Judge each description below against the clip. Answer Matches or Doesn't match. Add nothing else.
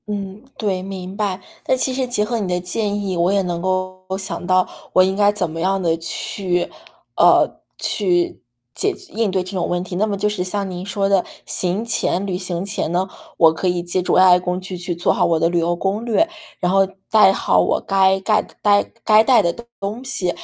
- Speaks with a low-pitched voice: Doesn't match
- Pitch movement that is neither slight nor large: Doesn't match